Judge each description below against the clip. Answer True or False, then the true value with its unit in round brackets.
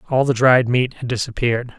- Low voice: True (125 Hz)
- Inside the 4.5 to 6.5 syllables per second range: True (6.0 syllables/s)